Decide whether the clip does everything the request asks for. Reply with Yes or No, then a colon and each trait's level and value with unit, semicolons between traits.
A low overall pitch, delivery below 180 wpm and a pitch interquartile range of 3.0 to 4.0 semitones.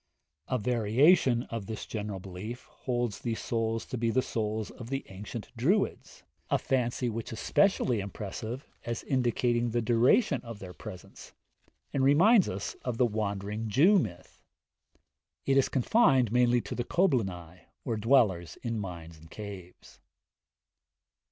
Yes: low, 115 Hz; average, 145 wpm; average, 3.6 semitones